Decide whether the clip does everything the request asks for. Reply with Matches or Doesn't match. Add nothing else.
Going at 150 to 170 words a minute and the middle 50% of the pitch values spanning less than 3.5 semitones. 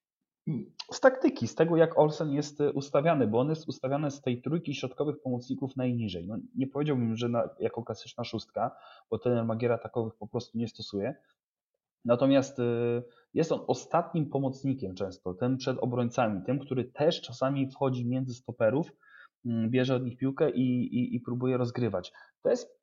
Matches